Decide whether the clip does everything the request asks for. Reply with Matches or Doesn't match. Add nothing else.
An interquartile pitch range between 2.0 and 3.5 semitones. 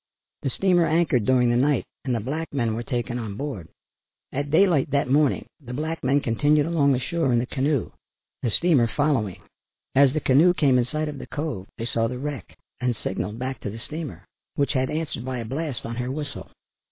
Doesn't match